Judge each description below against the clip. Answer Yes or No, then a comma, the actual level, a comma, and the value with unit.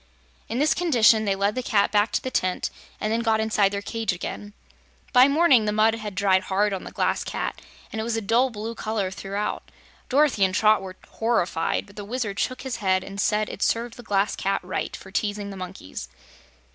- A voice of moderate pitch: No, high, 210 Hz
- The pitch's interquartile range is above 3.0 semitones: No, narrow, 2.5 semitones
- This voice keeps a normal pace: No, fast, 215 wpm